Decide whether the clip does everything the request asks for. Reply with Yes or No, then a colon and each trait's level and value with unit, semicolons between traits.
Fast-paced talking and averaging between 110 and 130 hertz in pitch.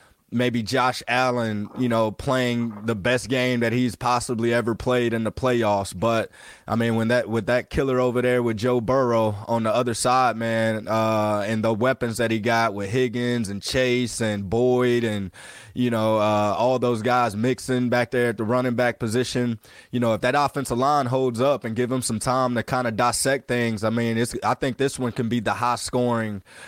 Yes: fast, 210 wpm; low, 120 Hz